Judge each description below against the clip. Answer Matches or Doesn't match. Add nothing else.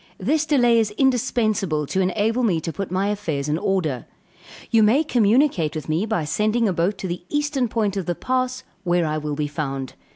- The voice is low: Doesn't match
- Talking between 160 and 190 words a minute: Doesn't match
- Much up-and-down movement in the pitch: Matches